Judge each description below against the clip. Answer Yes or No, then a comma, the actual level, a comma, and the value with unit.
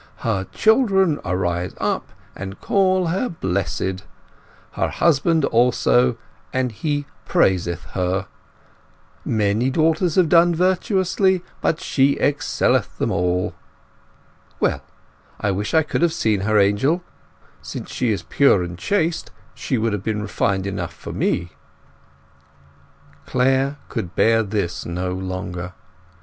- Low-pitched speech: Yes, low, 115 Hz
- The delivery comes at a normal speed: No, slow, 125 wpm